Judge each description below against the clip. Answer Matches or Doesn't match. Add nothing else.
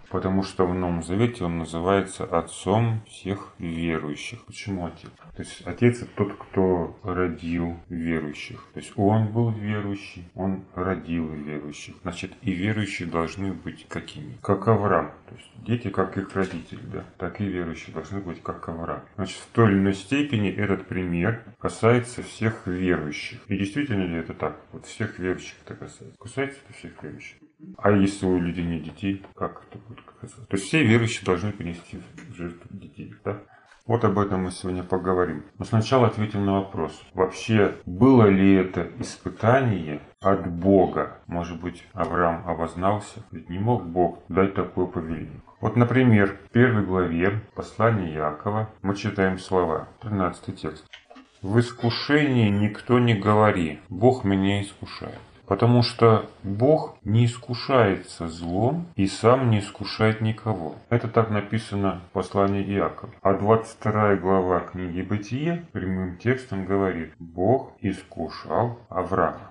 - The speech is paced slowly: Doesn't match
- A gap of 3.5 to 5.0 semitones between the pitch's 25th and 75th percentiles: Matches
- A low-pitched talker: Matches